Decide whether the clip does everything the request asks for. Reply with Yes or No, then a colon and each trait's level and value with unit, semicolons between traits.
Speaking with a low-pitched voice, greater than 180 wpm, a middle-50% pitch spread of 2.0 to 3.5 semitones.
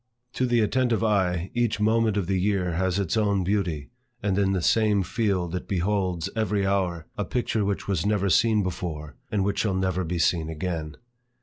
Yes: very low, 95 Hz; average, 190 wpm; average, 2.8 semitones